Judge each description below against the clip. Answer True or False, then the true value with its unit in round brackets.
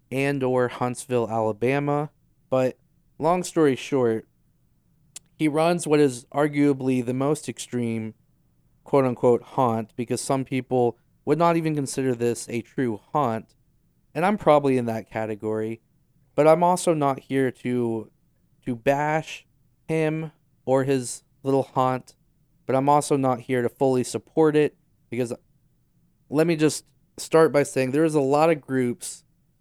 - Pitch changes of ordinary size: True (3.4 semitones)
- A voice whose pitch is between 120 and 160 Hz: True (135 Hz)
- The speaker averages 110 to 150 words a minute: True (140 wpm)